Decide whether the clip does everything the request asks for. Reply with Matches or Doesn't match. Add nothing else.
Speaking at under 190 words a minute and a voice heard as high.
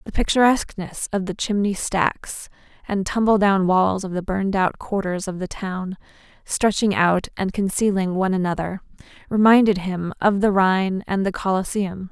Matches